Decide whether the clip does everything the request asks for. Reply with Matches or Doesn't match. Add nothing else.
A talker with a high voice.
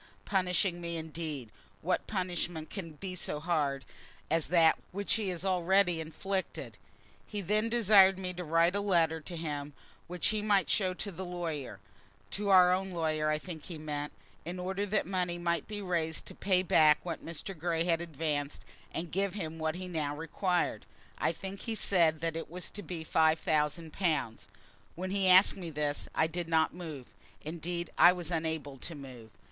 Doesn't match